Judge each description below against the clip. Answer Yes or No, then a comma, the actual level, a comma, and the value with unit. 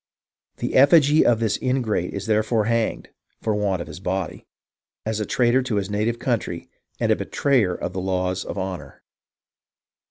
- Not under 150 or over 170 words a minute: Yes, average, 165 wpm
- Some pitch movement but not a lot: Yes, average, 4.0 semitones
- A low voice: Yes, low, 105 Hz